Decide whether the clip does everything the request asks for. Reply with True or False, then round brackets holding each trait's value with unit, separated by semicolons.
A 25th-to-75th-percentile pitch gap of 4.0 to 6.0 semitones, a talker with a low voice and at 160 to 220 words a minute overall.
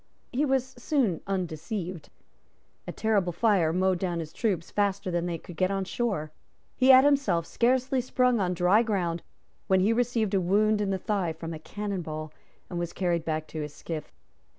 False (4.6 semitones; 190 Hz; 185 wpm)